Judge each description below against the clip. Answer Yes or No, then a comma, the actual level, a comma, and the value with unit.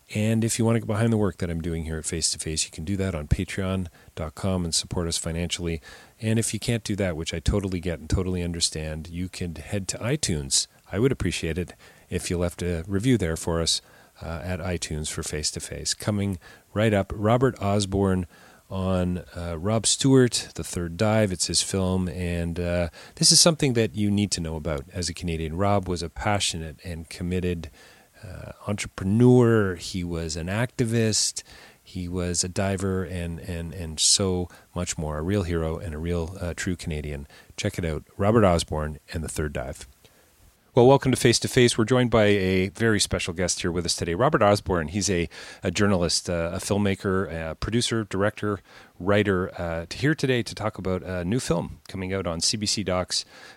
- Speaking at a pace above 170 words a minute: Yes, average, 200 wpm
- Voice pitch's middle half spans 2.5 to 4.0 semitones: Yes, average, 3.5 semitones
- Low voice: Yes, very low, 90 Hz